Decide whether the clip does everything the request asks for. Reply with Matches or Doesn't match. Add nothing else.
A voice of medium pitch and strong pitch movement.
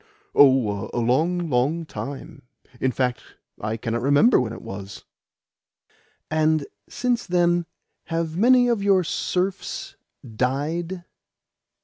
Matches